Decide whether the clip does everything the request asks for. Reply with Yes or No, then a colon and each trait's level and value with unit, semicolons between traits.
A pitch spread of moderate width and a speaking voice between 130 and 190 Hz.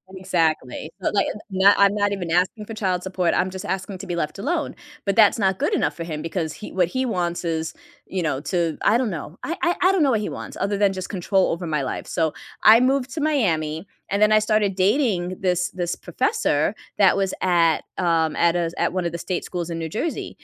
Yes: average, 3.8 semitones; medium, 185 Hz